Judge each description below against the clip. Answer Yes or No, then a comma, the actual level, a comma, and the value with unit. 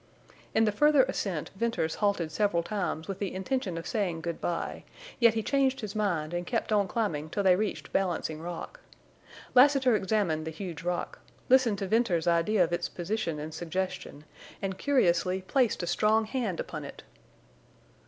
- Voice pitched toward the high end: Yes, high, 195 Hz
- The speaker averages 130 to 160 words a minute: No, average, 170 wpm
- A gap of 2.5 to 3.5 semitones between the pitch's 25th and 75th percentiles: No, average, 4.5 semitones